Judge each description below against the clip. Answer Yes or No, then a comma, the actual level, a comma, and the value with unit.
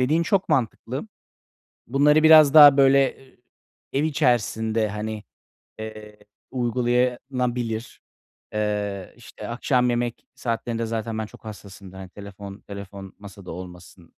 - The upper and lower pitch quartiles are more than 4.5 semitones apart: No, average, 3.9 semitones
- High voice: No, low, 115 Hz